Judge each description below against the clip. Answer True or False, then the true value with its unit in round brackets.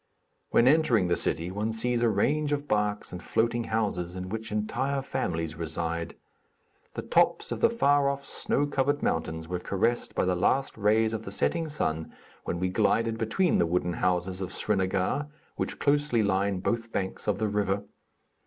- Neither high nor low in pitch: False (105 Hz)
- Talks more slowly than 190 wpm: True (175 wpm)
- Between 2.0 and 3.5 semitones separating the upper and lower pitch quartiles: False (5.2 semitones)